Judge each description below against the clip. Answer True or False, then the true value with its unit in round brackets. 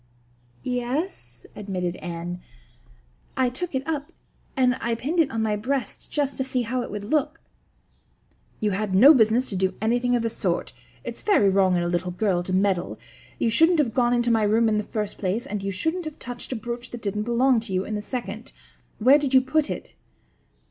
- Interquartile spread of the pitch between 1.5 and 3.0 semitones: False (4.7 semitones)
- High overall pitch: True (230 Hz)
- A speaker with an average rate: False (215 wpm)